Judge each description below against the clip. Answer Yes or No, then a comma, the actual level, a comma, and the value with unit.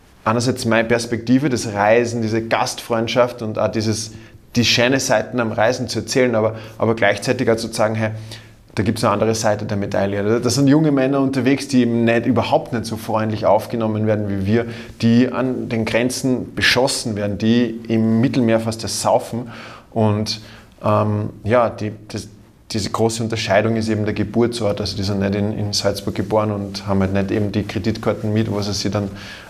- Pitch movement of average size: No, narrow, 1.9 semitones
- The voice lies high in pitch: No, low, 110 Hz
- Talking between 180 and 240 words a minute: Yes, average, 185 wpm